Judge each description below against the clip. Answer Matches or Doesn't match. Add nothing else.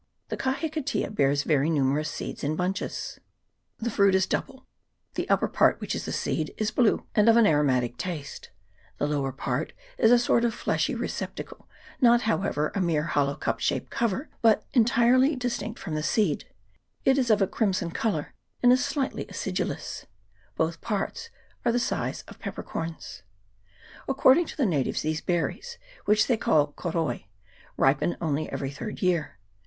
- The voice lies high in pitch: Matches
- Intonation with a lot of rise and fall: Matches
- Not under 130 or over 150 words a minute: Doesn't match